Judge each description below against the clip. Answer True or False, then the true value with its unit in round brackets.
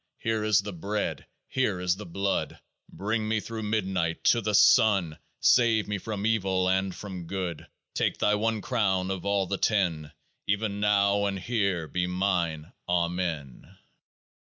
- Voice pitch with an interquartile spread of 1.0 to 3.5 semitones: True (2.7 semitones)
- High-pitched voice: False (100 Hz)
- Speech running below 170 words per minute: True (155 wpm)